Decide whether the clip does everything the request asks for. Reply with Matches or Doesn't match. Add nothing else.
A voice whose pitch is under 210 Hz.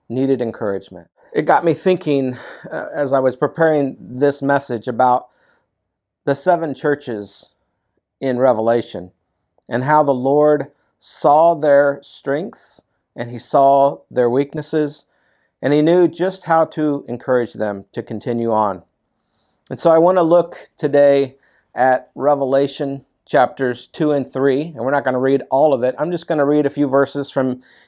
Matches